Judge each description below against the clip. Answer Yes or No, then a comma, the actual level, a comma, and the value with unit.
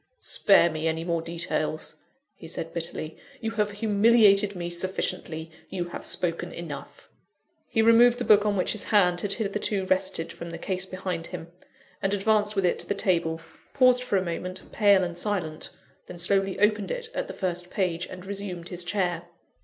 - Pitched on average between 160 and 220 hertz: Yes, medium, 185 Hz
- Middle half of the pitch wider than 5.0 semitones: No, average, 3.3 semitones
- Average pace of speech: Yes, average, 180 wpm